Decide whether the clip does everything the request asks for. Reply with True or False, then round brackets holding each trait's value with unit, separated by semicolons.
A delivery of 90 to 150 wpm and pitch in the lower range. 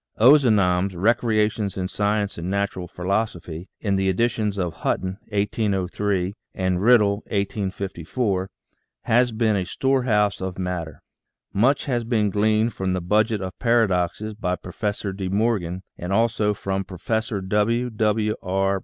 True (145 wpm; 100 Hz)